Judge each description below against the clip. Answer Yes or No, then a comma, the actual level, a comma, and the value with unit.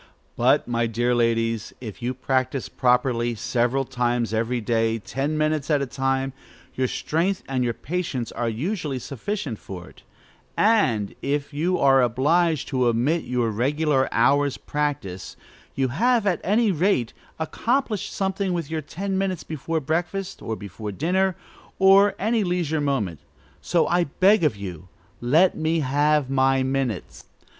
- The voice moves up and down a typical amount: No, wide, 5.9 semitones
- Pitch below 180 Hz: Yes, low, 135 Hz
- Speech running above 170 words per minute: No, average, 150 wpm